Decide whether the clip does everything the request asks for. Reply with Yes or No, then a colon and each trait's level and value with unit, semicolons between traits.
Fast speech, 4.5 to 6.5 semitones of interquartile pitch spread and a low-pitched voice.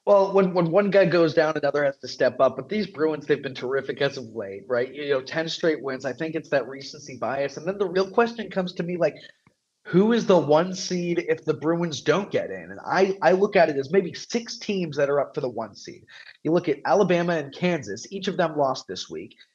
No: fast, 250 wpm; average, 5.2 semitones; medium, 165 Hz